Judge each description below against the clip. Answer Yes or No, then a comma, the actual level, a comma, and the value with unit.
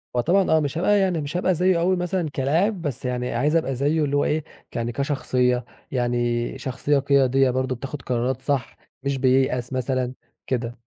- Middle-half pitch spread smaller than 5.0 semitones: Yes, average, 3.8 semitones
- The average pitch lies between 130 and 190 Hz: Yes, low, 135 Hz